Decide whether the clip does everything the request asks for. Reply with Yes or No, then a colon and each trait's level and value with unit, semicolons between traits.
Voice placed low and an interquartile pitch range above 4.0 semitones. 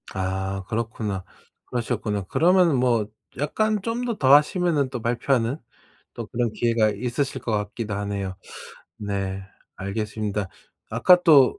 Yes: low, 115 Hz; wide, 5.6 semitones